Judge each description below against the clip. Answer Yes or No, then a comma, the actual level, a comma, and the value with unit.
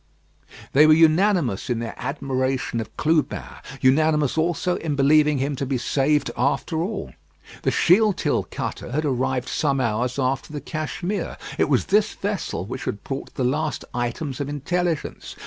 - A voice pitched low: No, medium, 145 Hz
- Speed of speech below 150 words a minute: No, average, 155 wpm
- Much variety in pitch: No, average, 3.5 semitones